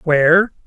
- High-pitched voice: No, medium, 170 Hz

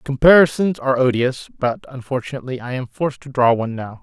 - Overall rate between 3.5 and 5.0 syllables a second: No, 6.4 syllables/s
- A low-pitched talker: Yes, low, 130 Hz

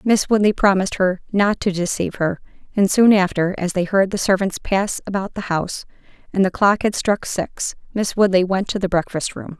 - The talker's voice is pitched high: Yes, high, 195 Hz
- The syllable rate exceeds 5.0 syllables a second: Yes, 5.3 syllables/s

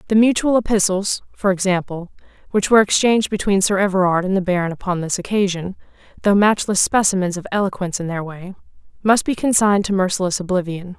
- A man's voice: No, female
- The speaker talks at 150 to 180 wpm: Yes, average, 170 wpm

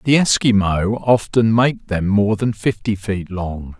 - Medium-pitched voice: No, low, 105 Hz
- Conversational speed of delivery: Yes, average, 160 wpm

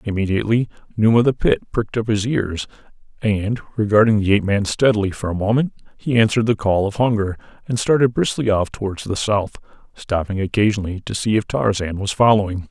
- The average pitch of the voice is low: Yes, low, 105 Hz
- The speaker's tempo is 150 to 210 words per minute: Yes, average, 185 wpm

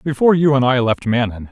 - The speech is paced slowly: No, fast, 240 wpm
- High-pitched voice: No, low, 130 Hz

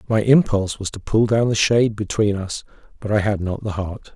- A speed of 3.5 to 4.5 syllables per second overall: No, 5.5 syllables/s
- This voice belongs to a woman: No, male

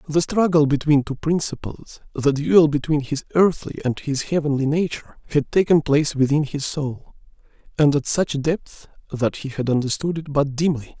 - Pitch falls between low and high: Yes, medium, 145 Hz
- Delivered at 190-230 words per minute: No, average, 165 wpm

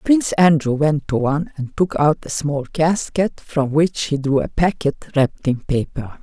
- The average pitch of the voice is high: No, medium, 150 Hz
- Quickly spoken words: No, average, 195 wpm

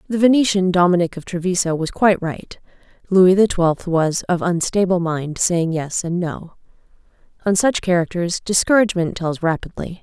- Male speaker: No, female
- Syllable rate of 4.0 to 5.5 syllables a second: Yes, 5.0 syllables/s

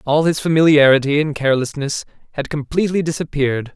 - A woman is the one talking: No, male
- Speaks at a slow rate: Yes, slow, 130 wpm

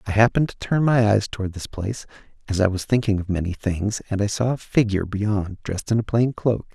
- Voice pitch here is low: Yes, low, 105 Hz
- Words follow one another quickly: Yes, fast, 240 wpm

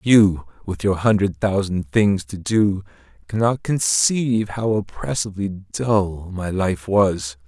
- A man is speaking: Yes, male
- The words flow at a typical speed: No, slow, 130 wpm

